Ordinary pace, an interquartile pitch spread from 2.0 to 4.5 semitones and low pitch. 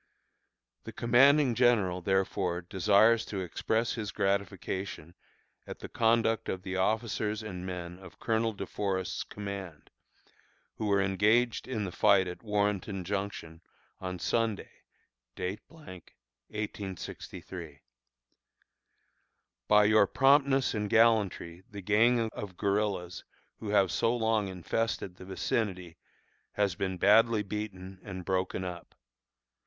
No: slow, 115 wpm; average, 3.1 semitones; low, 100 Hz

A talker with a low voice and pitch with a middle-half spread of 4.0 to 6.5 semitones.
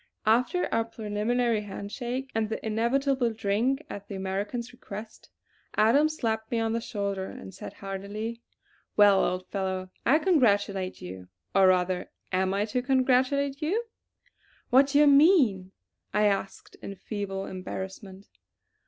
No: high, 215 Hz; average, 4.3 semitones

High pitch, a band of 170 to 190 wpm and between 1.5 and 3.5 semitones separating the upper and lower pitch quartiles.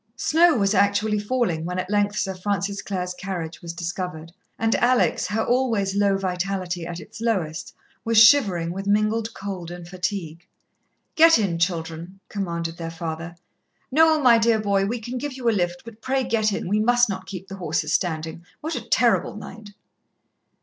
No: high, 195 Hz; average, 175 wpm; average, 4.3 semitones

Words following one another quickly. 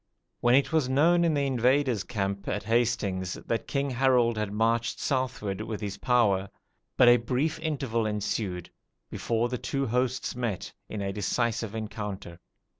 No: average, 150 wpm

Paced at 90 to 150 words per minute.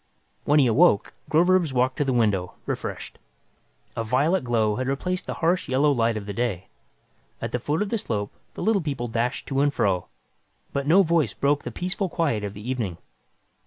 No: average, 190 wpm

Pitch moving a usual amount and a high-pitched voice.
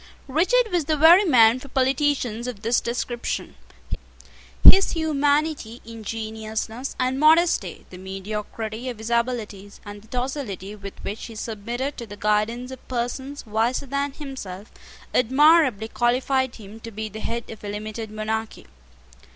Yes: average, 3.9 semitones; high, 235 Hz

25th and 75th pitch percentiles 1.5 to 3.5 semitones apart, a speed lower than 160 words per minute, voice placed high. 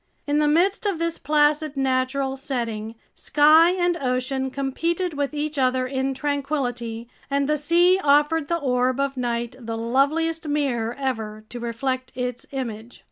Yes: average, 3.2 semitones; average, 150 wpm; very high, 275 Hz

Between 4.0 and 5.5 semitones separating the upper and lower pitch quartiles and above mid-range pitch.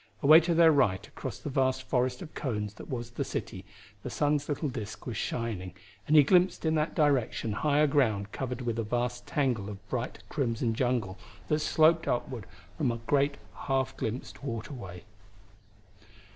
No: average, 4.3 semitones; low, 130 Hz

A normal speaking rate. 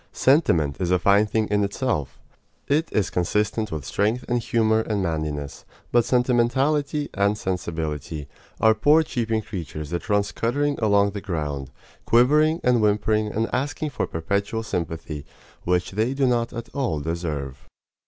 Yes: average, 150 wpm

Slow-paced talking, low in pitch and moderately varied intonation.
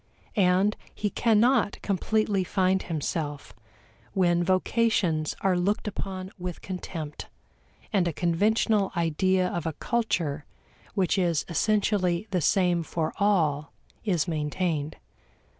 No: slow, 110 wpm; medium, 180 Hz; average, 3.4 semitones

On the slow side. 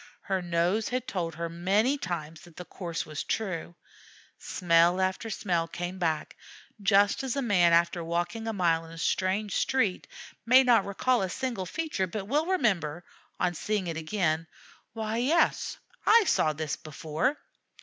No: average, 160 wpm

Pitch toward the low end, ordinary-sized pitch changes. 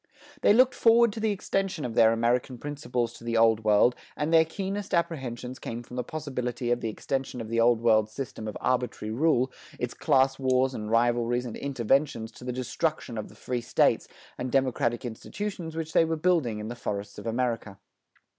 Yes: low, 125 Hz; average, 4.9 semitones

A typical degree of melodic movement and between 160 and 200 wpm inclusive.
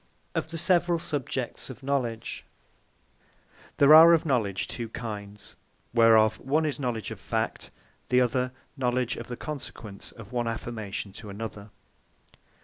No: average, 4.1 semitones; average, 140 wpm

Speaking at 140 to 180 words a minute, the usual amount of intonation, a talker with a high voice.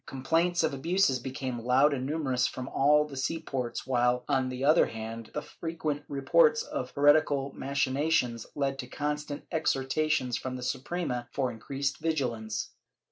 No: average, 155 wpm; average, 3.1 semitones; low, 135 Hz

